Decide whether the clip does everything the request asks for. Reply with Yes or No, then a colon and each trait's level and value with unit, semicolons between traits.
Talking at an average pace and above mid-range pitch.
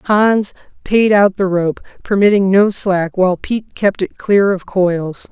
Yes: average, 170 wpm; high, 195 Hz